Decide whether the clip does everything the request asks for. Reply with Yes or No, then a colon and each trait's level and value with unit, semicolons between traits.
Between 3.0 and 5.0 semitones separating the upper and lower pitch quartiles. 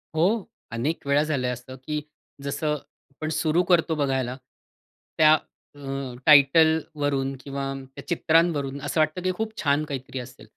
No: narrow, 2.6 semitones